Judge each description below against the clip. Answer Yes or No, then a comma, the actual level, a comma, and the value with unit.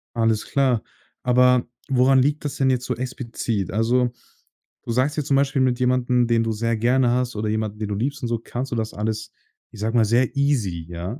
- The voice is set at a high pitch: No, low, 120 Hz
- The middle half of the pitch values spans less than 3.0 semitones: Yes, narrow, 2.6 semitones